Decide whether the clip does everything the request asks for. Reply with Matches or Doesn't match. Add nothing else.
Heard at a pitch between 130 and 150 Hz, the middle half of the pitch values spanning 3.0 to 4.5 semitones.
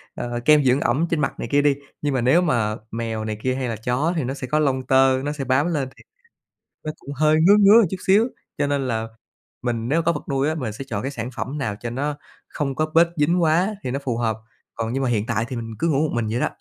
Matches